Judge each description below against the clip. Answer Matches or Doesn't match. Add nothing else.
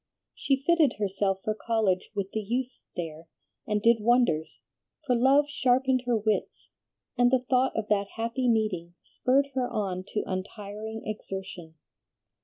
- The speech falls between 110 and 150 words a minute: Matches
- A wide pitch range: Doesn't match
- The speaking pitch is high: Matches